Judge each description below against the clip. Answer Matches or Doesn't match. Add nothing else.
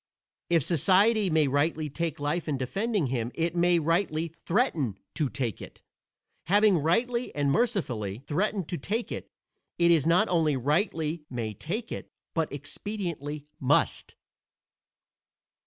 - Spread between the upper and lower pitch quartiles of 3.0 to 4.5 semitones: Doesn't match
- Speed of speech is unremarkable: Doesn't match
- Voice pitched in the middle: Matches